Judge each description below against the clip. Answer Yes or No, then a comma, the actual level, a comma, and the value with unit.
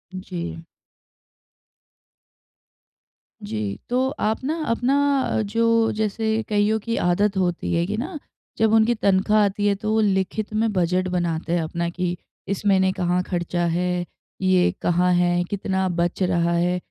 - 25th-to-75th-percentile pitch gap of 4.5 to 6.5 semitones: No, average, 3.7 semitones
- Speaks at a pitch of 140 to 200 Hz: Yes, high, 190 Hz